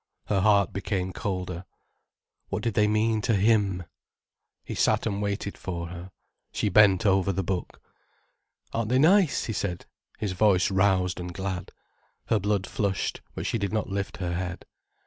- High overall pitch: No, low, 100 Hz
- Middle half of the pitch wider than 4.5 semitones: No, narrow, 2.5 semitones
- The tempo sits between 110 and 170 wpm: Yes, average, 165 wpm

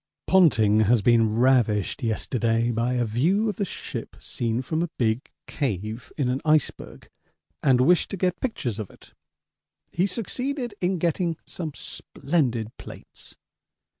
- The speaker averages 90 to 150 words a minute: Yes, average, 140 wpm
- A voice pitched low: Yes, low, 130 Hz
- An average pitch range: No, wide, 7.3 semitones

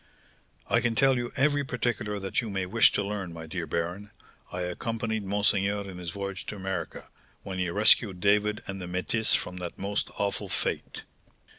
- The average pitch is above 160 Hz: No, low, 100 Hz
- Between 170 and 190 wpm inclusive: Yes, average, 180 wpm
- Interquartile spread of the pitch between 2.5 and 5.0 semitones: Yes, average, 2.8 semitones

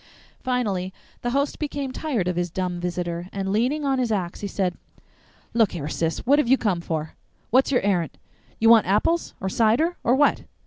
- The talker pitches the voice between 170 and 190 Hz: No, high, 210 Hz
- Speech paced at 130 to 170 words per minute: No, average, 195 wpm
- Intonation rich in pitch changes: Yes, wide, 6.4 semitones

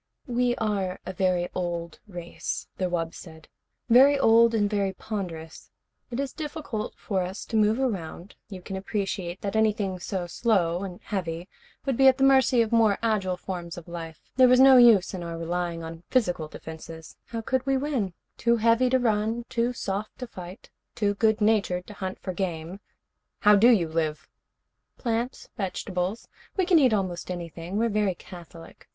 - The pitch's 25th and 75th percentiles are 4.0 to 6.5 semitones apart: Yes, average, 4.8 semitones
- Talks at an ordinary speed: Yes, average, 180 wpm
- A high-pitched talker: Yes, high, 200 Hz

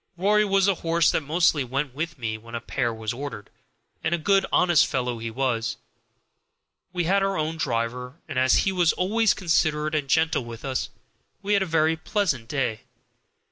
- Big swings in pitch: Yes, wide, 6.0 semitones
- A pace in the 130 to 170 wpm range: No, average, 185 wpm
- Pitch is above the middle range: No, medium, 155 Hz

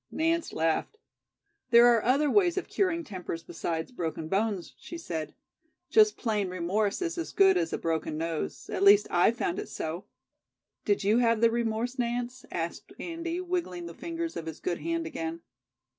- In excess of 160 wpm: Yes, average, 175 wpm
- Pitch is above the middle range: Yes, high, 230 Hz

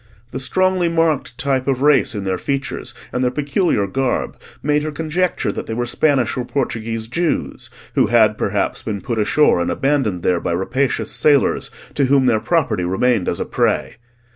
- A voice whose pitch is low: Yes, low, 130 Hz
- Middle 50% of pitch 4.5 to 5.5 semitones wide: Yes, average, 5.0 semitones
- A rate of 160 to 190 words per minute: Yes, average, 180 wpm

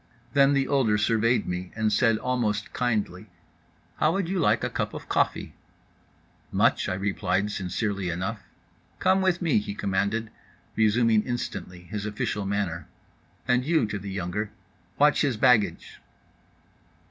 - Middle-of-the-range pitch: No, low, 105 Hz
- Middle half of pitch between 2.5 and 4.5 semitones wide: Yes, average, 4.0 semitones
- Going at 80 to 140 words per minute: Yes, slow, 135 wpm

